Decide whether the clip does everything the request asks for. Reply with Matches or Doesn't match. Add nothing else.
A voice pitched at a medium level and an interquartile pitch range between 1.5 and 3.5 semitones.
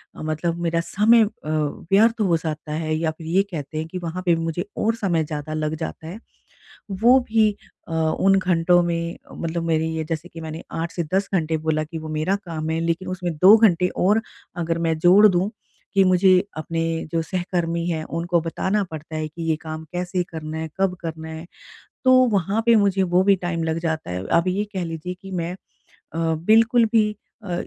Matches